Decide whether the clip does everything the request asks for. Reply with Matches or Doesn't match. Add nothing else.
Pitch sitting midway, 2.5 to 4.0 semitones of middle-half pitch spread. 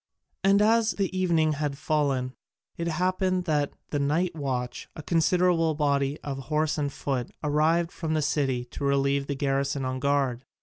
Matches